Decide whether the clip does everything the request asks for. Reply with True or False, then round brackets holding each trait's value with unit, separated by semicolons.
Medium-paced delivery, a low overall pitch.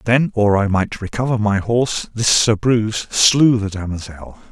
True (185 wpm; 110 Hz)